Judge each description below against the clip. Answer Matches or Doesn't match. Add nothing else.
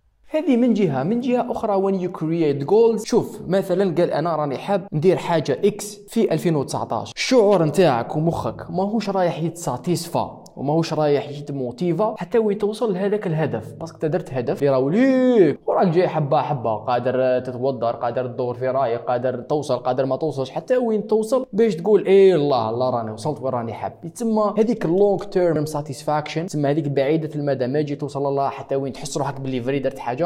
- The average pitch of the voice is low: Doesn't match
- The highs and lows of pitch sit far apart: Matches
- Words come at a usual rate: Doesn't match